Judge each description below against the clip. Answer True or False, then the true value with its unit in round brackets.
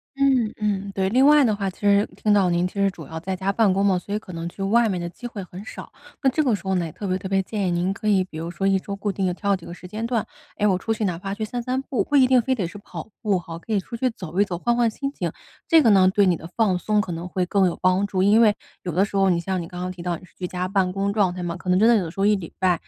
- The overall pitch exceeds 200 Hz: False (195 Hz)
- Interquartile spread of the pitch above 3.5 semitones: False (2.9 semitones)